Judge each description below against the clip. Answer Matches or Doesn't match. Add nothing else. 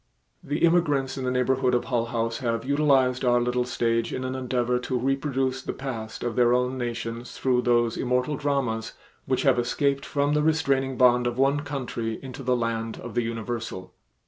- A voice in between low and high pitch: Doesn't match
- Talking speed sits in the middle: Matches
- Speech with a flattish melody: Matches